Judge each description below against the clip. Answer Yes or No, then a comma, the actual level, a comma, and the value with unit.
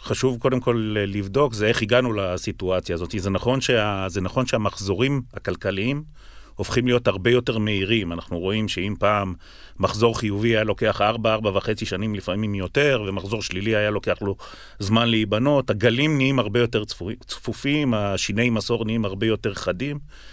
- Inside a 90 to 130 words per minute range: No, fast, 150 wpm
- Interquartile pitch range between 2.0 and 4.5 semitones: Yes, average, 3.5 semitones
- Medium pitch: No, low, 110 Hz